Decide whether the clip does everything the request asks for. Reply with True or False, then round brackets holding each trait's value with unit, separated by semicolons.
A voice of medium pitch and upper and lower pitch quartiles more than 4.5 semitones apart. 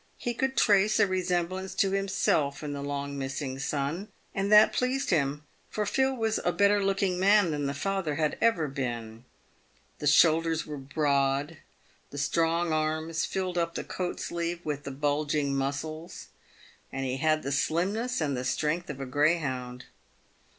True (155 Hz; 5.0 semitones)